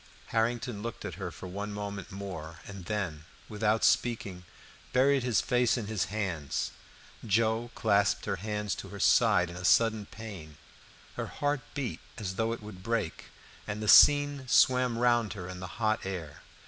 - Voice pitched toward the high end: No, low, 105 Hz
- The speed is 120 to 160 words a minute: No, average, 175 wpm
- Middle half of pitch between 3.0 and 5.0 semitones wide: Yes, average, 3.7 semitones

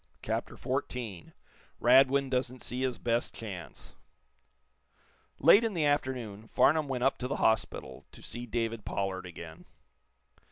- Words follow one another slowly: Yes, slow, 130 wpm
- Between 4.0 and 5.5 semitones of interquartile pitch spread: No, average, 3.5 semitones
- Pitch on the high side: No, low, 125 Hz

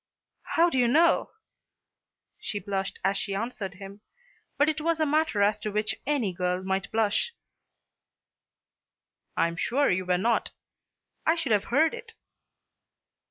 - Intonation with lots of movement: Yes, wide, 7.6 semitones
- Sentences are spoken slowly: No, average, 150 wpm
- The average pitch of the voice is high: Yes, high, 215 Hz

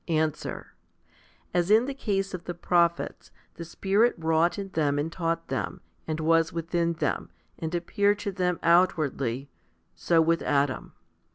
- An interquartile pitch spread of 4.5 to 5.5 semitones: No, narrow, 2.4 semitones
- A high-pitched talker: No, medium, 170 Hz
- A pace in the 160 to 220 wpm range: No, average, 150 wpm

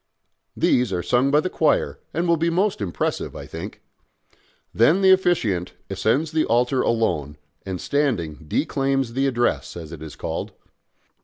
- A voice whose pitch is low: Yes, low, 125 Hz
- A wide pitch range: Yes, wide, 8.5 semitones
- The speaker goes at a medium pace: Yes, average, 155 wpm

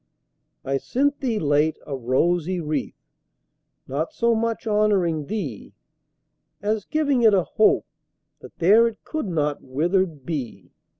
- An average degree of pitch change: No, wide, 7.0 semitones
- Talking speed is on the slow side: Yes, slow, 130 wpm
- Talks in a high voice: No, medium, 175 Hz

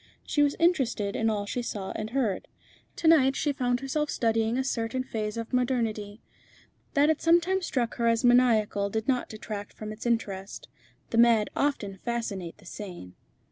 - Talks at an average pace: Yes, average, 175 wpm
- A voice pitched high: Yes, high, 230 Hz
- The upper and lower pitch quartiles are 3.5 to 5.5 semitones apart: Yes, average, 3.8 semitones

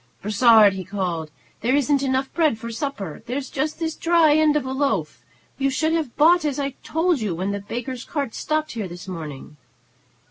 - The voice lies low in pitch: No, very high, 260 Hz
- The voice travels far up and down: Yes, wide, 6.8 semitones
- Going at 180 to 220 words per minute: Yes, average, 190 wpm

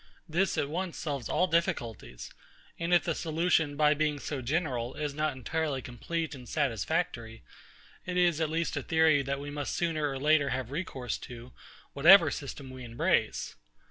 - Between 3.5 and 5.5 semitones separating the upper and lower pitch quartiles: Yes, average, 3.8 semitones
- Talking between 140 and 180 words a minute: Yes, average, 170 wpm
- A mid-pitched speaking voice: Yes, medium, 150 Hz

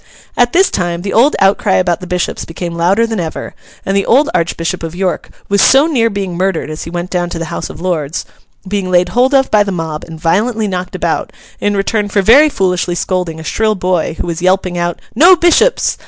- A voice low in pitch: No, medium, 185 Hz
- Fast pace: Yes, fast, 215 wpm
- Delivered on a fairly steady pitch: No, average, 3.8 semitones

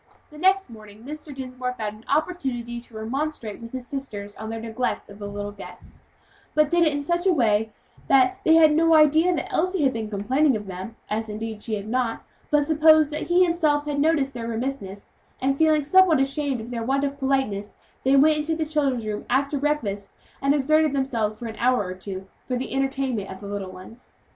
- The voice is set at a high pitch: Yes, very high, 265 Hz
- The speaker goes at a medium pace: No, fast, 210 wpm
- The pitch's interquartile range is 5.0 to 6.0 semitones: Yes, wide, 5.5 semitones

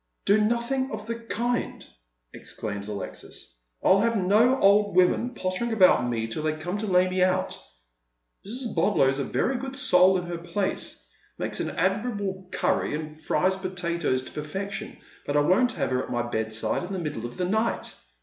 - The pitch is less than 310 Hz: Yes, medium, 185 Hz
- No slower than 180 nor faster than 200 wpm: Yes, average, 190 wpm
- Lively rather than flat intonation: Yes, wide, 6.0 semitones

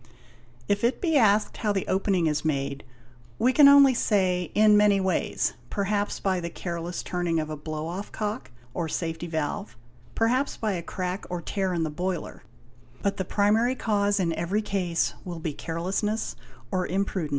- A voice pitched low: No, high, 190 Hz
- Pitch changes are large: No, average, 3.7 semitones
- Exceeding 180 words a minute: No, average, 175 wpm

